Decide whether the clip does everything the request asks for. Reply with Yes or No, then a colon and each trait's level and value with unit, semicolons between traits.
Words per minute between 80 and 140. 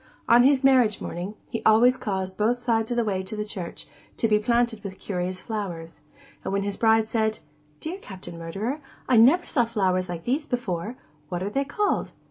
No: average, 190 wpm